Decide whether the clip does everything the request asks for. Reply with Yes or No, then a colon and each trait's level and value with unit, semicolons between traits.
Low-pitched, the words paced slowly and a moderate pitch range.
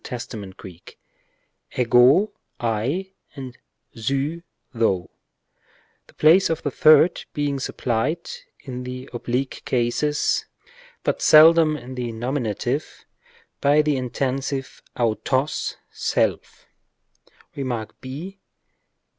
Yes: low, 130 Hz; slow, 95 wpm; average, 3.9 semitones